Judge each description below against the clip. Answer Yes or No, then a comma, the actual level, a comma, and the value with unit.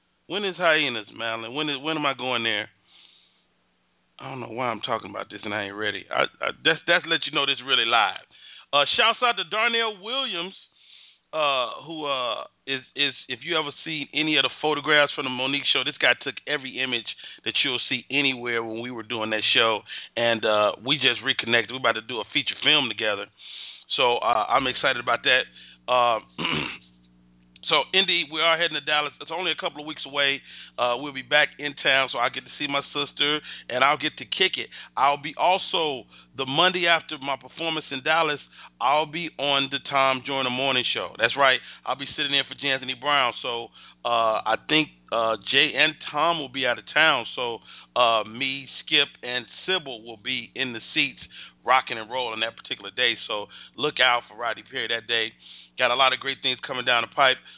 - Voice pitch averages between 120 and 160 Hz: Yes, low, 135 Hz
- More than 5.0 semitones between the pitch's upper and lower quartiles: No, average, 4.2 semitones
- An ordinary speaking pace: No, fast, 210 wpm